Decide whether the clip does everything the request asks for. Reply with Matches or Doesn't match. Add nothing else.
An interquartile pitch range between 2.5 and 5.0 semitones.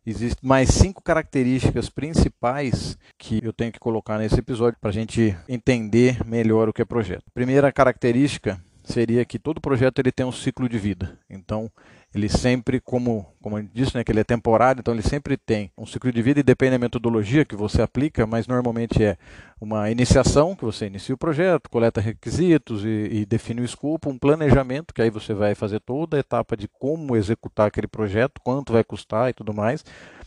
Matches